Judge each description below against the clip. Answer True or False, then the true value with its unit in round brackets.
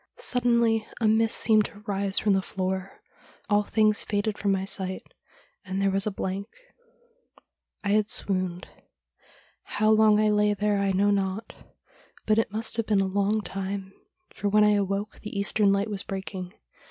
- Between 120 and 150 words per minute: False (175 wpm)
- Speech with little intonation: True (1.7 semitones)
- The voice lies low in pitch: False (205 Hz)